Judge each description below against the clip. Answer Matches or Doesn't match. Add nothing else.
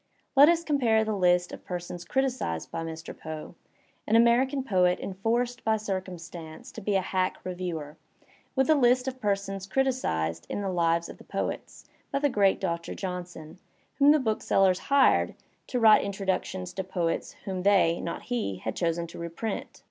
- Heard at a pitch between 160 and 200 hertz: Matches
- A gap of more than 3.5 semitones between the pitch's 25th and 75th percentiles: Matches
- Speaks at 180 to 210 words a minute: Doesn't match